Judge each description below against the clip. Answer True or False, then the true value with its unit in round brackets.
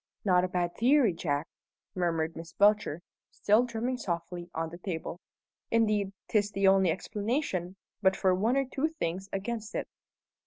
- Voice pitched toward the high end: True (195 Hz)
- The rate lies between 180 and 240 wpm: False (155 wpm)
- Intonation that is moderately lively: True (4.2 semitones)